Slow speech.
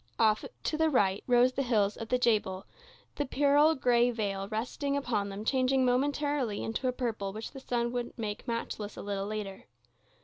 No: average, 180 wpm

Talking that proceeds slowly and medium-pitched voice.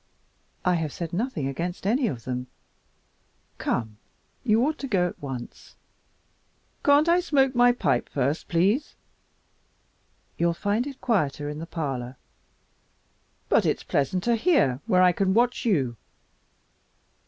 Yes: slow, 130 wpm; medium, 180 Hz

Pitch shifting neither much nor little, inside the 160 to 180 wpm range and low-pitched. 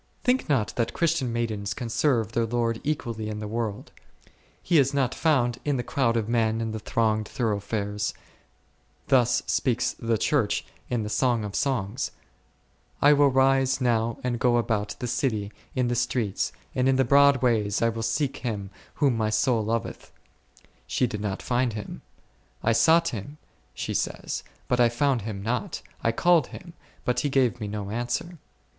Yes: average, 3.3 semitones; average, 175 wpm; low, 120 Hz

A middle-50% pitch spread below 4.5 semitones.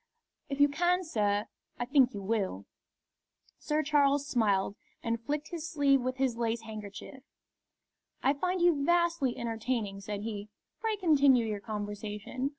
No: wide, 5.5 semitones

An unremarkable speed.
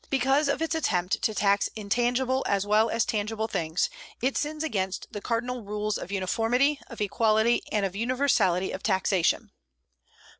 Yes: average, 155 wpm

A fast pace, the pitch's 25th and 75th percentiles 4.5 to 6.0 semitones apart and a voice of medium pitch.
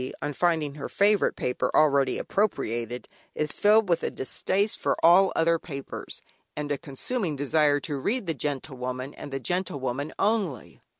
No: average, 155 wpm; average, 5.1 semitones; medium, 150 Hz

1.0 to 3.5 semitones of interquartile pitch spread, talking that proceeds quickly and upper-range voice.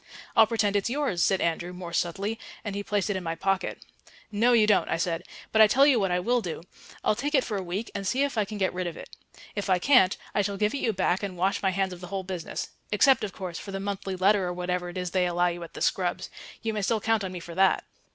Yes: average, 3.0 semitones; fast, 280 wpm; high, 195 Hz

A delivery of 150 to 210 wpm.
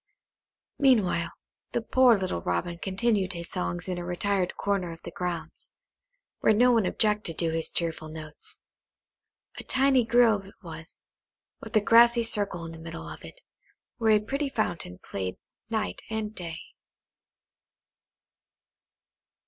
No: average, 140 wpm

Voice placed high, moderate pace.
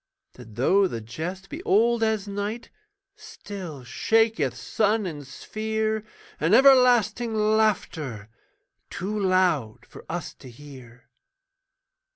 No: high, 195 Hz; slow, 110 wpm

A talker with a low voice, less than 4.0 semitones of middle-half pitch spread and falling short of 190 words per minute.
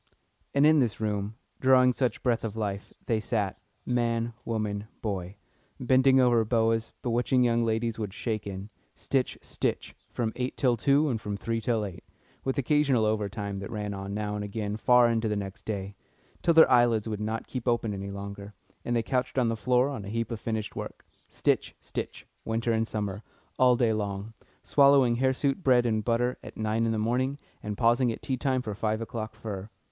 No: low, 115 Hz; average, 2.9 semitones; average, 195 wpm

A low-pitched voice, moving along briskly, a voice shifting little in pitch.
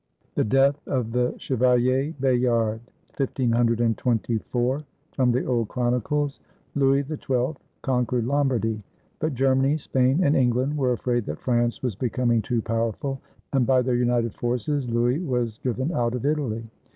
No: low, 125 Hz; slow, 135 wpm; narrow, 2.2 semitones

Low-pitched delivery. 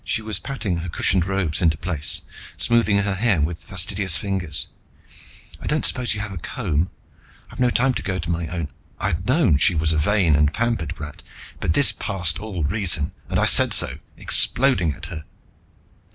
Yes: very low, 90 Hz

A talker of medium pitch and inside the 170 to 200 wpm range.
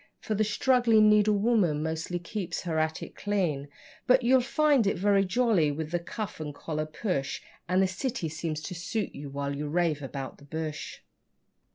Yes: medium, 175 Hz; average, 175 wpm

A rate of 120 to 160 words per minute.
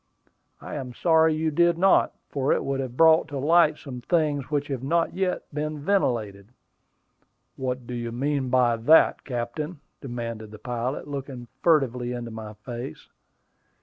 Yes: average, 155 wpm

